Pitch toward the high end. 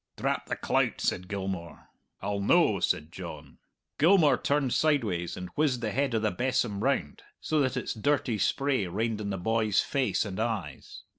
No: low, 110 Hz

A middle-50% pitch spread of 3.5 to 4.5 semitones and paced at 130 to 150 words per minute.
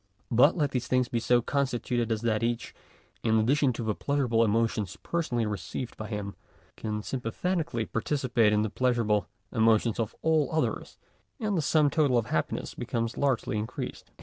No: average, 3.9 semitones; average, 170 wpm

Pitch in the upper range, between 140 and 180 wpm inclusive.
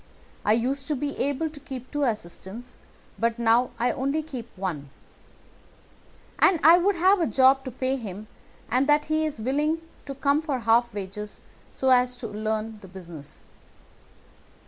Yes: very high, 255 Hz; average, 165 wpm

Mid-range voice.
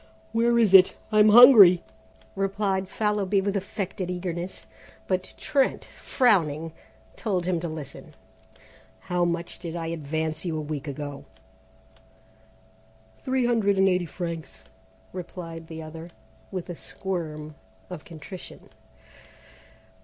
Yes: medium, 180 Hz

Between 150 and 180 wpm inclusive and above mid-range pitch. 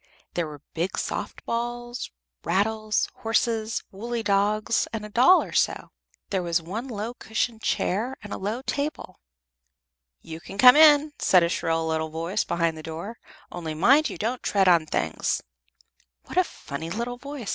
Yes: average, 165 wpm; high, 215 Hz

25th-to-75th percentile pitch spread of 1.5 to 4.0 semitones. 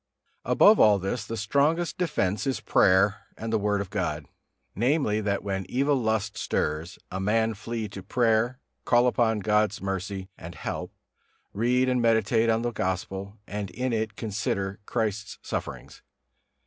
Yes: average, 3.1 semitones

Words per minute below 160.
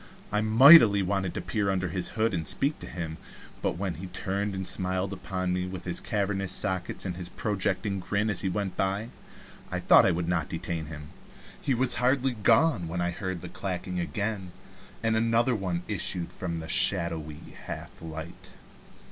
No: average, 180 wpm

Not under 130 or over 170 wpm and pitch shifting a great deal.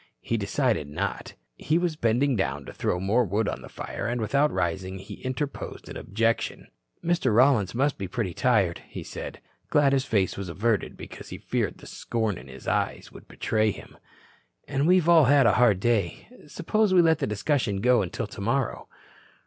No: average, 185 wpm; wide, 6.0 semitones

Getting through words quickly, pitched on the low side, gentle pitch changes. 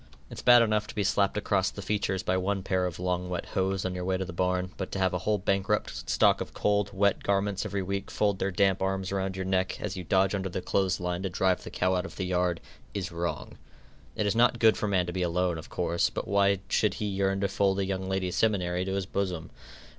Yes: fast, 250 wpm; very low, 95 Hz; narrow, 1.5 semitones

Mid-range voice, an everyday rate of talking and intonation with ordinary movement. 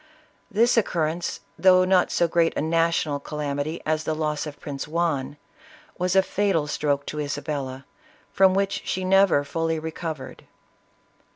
Yes: medium, 160 Hz; average, 155 wpm; average, 3.8 semitones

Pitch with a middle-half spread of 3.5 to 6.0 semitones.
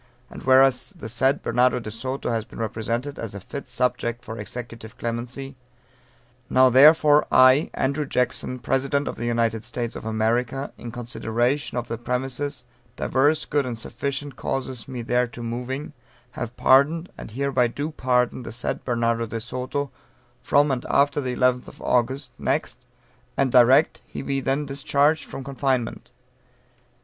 No: average, 2.7 semitones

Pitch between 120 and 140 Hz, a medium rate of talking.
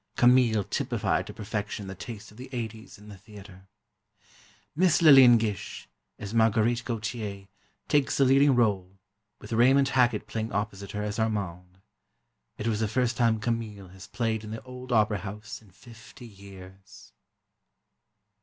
No: low, 110 Hz; average, 150 wpm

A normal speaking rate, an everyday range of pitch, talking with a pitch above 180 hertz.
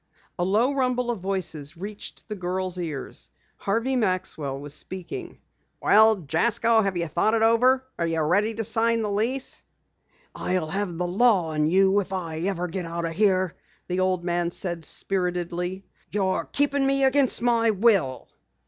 Yes: average, 165 wpm; average, 4.6 semitones; high, 190 Hz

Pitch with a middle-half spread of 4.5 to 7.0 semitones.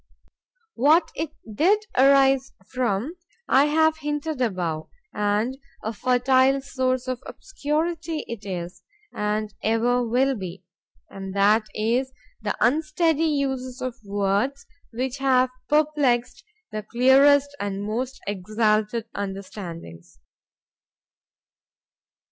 Yes: average, 5.2 semitones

